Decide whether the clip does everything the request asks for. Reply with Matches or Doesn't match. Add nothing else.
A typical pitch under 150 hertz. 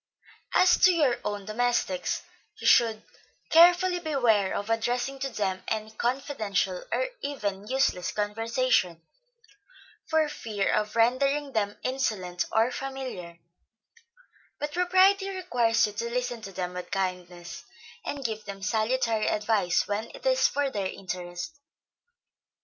Doesn't match